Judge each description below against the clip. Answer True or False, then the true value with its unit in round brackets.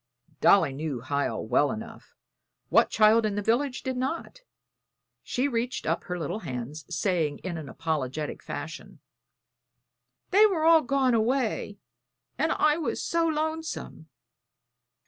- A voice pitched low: False (215 Hz)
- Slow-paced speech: True (130 wpm)